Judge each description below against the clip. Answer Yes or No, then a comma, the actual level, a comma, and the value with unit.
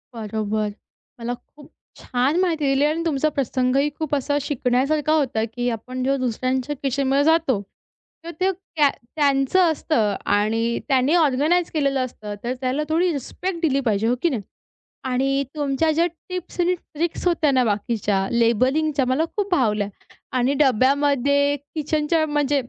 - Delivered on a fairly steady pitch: No, average, 3.8 semitones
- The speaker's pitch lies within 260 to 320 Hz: Yes, very high, 275 Hz